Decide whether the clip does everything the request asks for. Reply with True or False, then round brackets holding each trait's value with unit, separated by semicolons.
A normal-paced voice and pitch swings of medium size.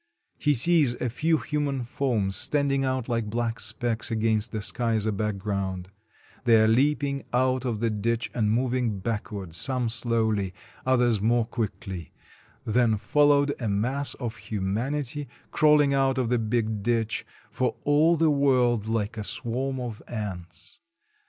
True (150 wpm; 3.5 semitones)